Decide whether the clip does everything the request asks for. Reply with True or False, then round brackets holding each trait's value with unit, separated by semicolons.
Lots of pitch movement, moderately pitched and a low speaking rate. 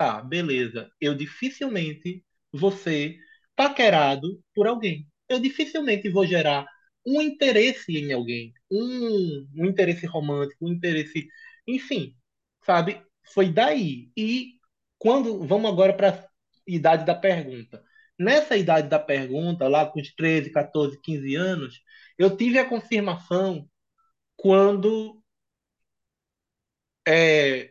True (6.4 semitones; 180 Hz; 115 wpm)